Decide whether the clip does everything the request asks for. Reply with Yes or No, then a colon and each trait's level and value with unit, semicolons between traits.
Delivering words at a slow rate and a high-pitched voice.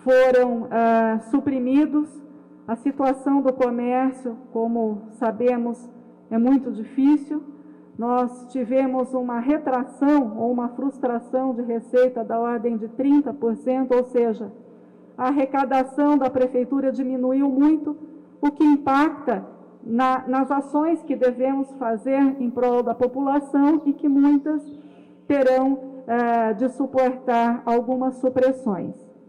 Yes: slow, 115 wpm; very high, 255 Hz